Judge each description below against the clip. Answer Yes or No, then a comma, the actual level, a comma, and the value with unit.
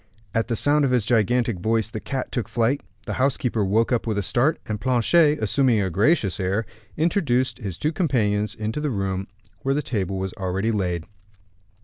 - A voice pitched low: Yes, low, 115 Hz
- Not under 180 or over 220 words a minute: Yes, average, 190 wpm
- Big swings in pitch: No, average, 4.5 semitones